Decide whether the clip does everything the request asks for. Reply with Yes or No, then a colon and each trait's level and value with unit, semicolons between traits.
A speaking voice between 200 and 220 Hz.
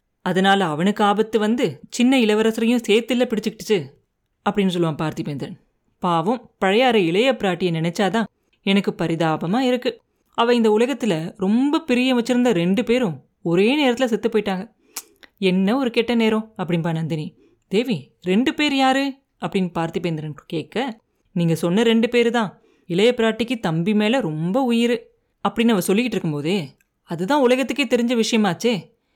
Yes: high, 215 Hz